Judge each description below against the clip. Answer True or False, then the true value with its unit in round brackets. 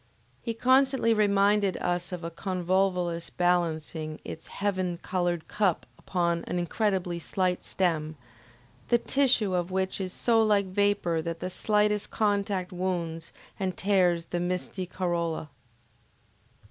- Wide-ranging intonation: False (2.7 semitones)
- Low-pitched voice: False (185 Hz)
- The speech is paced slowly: True (125 wpm)